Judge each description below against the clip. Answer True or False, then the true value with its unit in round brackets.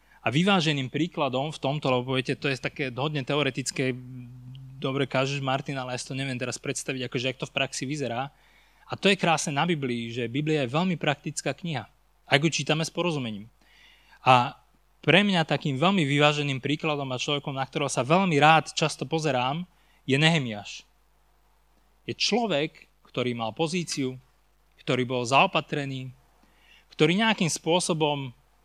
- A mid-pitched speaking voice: True (145 Hz)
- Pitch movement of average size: True (3.2 semitones)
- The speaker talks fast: False (155 wpm)